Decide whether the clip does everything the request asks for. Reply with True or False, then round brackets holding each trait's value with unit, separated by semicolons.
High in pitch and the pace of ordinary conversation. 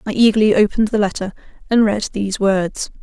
True (205 Hz; 180 wpm)